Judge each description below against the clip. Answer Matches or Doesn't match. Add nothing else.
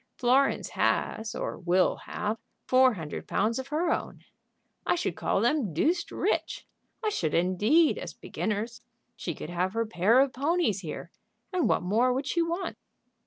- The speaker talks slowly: Doesn't match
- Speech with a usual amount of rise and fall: Doesn't match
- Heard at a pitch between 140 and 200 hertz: Doesn't match